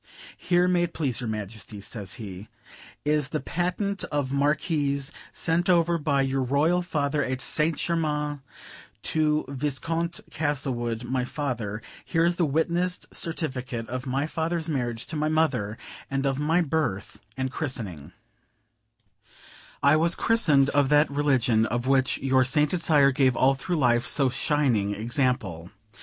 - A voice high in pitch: No, medium, 140 Hz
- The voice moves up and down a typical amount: Yes, average, 4.1 semitones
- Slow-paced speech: No, average, 145 wpm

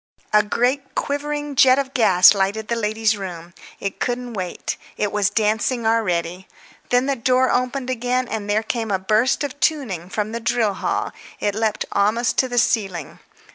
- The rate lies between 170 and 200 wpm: Yes, average, 175 wpm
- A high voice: Yes, high, 225 Hz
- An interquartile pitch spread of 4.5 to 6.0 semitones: No, average, 3.8 semitones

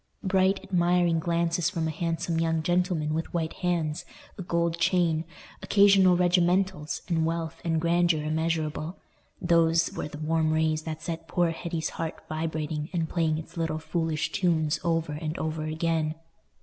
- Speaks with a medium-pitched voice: Yes, medium, 165 Hz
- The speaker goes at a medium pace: Yes, average, 150 wpm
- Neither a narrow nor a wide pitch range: No, narrow, 1.6 semitones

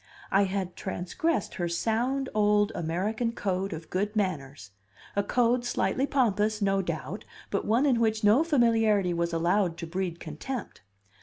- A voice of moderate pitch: No, high, 205 Hz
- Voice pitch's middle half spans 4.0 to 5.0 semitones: Yes, average, 4.5 semitones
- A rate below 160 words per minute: Yes, average, 150 wpm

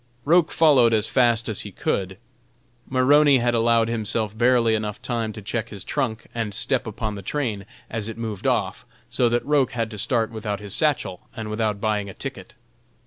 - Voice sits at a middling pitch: No, low, 115 Hz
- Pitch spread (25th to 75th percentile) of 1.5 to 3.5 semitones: Yes, average, 2.7 semitones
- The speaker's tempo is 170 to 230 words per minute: Yes, average, 190 wpm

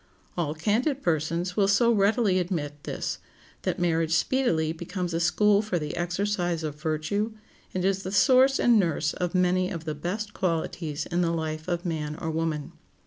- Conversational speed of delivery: Yes, average, 175 wpm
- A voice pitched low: No, medium, 175 Hz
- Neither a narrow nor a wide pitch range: Yes, average, 3.8 semitones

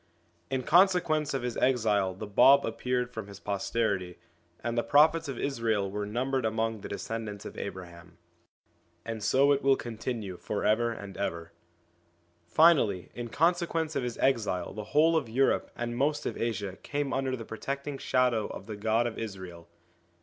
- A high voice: No, low, 115 Hz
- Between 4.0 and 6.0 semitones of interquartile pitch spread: Yes, average, 4.8 semitones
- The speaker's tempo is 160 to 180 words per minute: Yes, average, 170 wpm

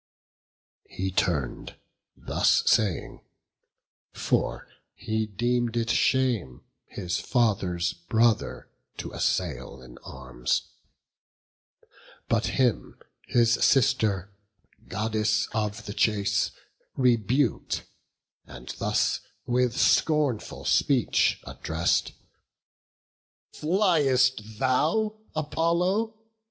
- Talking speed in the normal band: No, slow, 75 wpm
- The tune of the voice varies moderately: Yes, average, 4.8 semitones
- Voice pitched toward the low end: Yes, low, 115 Hz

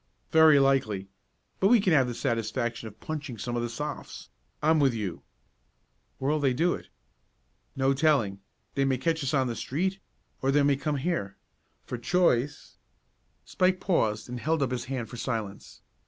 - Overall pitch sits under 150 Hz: Yes, low, 135 Hz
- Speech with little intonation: No, average, 4.6 semitones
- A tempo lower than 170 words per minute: No, average, 175 wpm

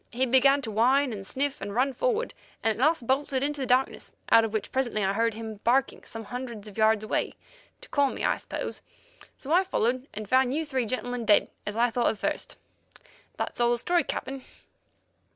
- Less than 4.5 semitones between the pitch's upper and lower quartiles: Yes, average, 3.4 semitones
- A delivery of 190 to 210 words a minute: Yes, fast, 205 wpm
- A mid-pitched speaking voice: No, high, 245 Hz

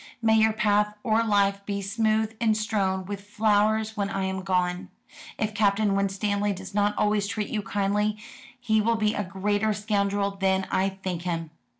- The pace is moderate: Yes, average, 175 wpm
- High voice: Yes, high, 205 Hz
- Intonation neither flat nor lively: No, narrow, 1.7 semitones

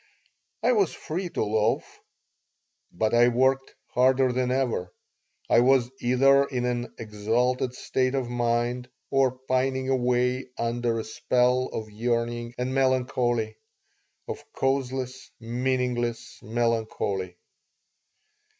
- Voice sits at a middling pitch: No, low, 125 Hz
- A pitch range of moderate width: No, narrow, 1.8 semitones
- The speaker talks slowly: Yes, slow, 110 wpm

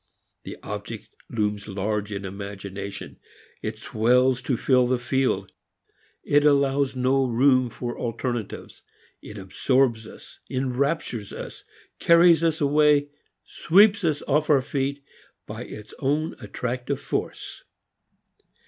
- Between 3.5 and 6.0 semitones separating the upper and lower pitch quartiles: Yes, average, 4.7 semitones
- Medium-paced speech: No, slow, 115 wpm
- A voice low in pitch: Yes, low, 130 Hz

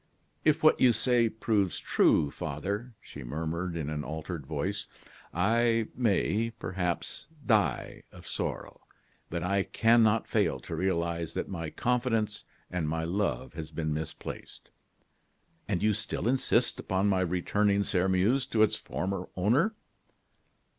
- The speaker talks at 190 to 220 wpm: No, slow, 135 wpm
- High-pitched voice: No, very low, 95 Hz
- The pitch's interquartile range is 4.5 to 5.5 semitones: Yes, average, 5.1 semitones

